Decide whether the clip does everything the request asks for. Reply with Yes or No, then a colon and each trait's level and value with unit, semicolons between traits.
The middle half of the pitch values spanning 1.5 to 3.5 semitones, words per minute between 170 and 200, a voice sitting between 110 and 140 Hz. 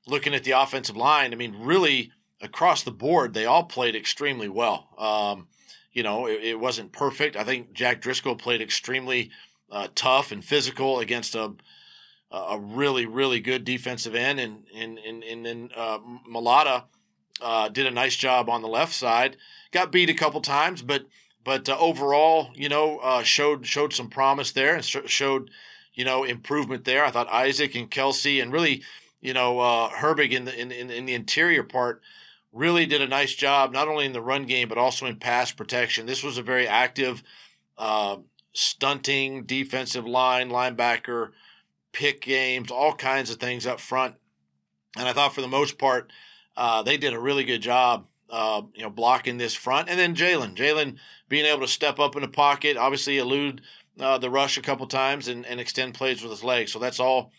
Yes: narrow, 2.6 semitones; average, 190 wpm; low, 130 Hz